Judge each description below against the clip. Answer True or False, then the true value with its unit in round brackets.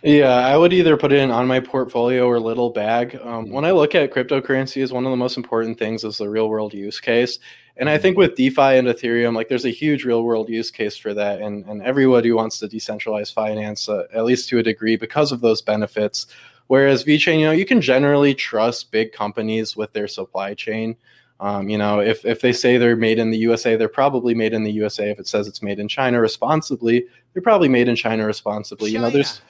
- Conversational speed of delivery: False (230 wpm)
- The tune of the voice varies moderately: True (3.0 semitones)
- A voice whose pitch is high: False (115 Hz)